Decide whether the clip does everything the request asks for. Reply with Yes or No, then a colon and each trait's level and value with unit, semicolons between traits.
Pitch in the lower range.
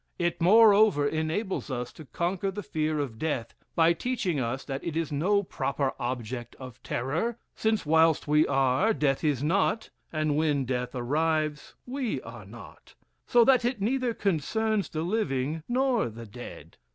No: medium, 155 Hz